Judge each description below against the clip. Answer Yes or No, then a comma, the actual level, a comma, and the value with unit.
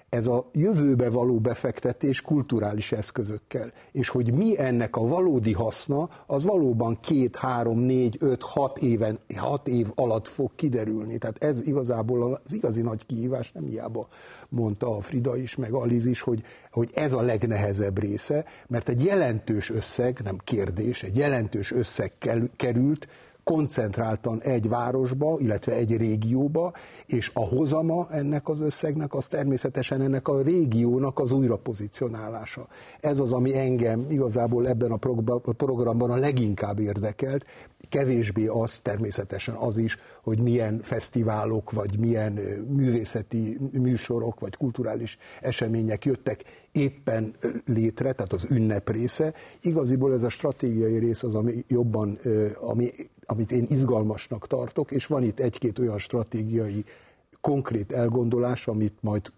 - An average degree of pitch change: Yes, average, 3.0 semitones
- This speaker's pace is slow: No, average, 135 wpm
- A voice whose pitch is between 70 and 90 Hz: No, low, 120 Hz